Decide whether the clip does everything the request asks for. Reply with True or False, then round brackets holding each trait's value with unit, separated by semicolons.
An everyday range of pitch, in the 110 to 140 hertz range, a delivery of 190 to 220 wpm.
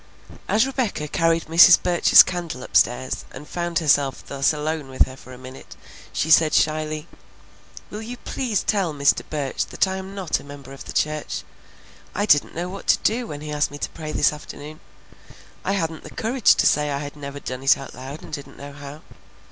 False (3.6 semitones; 155 Hz; 200 wpm)